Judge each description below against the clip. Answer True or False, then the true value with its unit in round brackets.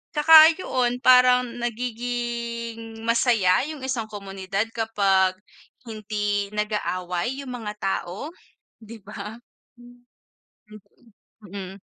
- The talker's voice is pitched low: False (225 Hz)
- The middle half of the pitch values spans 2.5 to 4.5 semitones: True (3.3 semitones)